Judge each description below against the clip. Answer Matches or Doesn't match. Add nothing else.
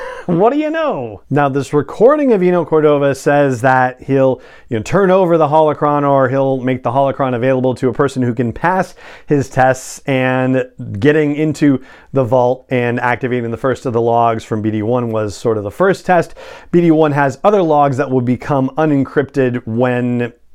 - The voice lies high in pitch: Doesn't match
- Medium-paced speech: Matches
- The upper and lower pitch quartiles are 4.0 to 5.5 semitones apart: Doesn't match